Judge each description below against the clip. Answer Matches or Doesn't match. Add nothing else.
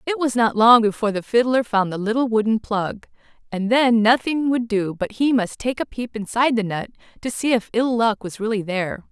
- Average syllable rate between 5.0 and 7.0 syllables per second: Matches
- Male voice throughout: Doesn't match